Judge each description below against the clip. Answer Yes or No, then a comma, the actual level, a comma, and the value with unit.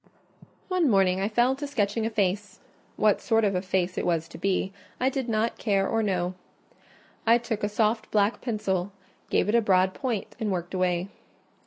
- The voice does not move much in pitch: No, average, 3.3 semitones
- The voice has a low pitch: No, high, 205 Hz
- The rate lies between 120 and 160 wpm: No, average, 190 wpm